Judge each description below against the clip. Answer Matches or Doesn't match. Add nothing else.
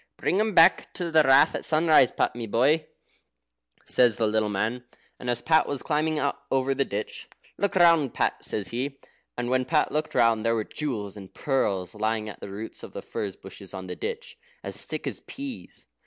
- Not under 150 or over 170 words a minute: Doesn't match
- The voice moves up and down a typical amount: Doesn't match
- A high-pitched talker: Doesn't match